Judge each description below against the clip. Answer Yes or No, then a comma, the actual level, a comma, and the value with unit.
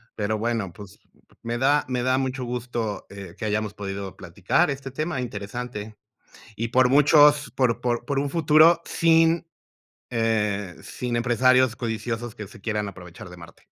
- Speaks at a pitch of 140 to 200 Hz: No, low, 120 Hz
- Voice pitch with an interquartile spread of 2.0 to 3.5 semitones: No, average, 4.2 semitones